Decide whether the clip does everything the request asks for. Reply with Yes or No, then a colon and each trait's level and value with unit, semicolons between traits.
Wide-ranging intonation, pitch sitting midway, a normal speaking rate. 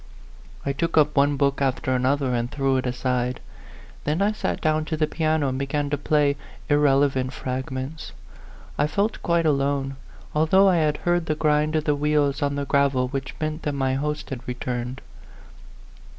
No: narrow, 2.5 semitones; medium, 145 Hz; average, 175 wpm